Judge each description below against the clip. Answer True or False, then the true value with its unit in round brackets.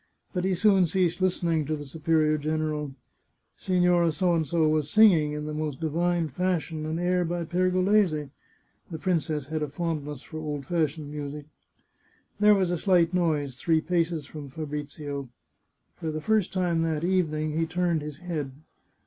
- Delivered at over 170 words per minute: False (160 wpm)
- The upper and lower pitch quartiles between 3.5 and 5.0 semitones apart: False (2.8 semitones)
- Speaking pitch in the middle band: True (160 Hz)